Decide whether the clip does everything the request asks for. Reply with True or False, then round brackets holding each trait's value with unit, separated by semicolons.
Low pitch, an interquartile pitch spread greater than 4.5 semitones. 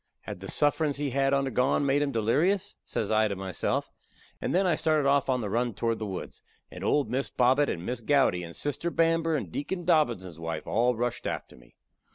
True (130 Hz; 5.3 semitones)